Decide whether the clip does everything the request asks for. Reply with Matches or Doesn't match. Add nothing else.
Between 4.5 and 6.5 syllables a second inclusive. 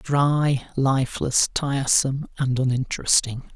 Doesn't match